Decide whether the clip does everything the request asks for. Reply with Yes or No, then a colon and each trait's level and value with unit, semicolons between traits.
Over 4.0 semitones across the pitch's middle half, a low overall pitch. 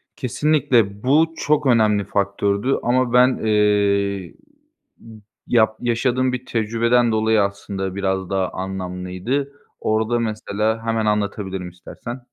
No: average, 3.5 semitones; low, 110 Hz